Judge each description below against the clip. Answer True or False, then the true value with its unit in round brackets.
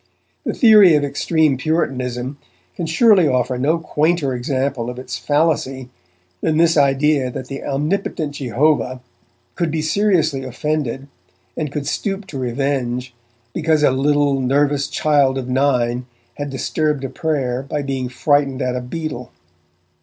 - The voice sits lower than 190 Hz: True (140 Hz)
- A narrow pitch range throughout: False (3.2 semitones)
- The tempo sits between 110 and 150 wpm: True (140 wpm)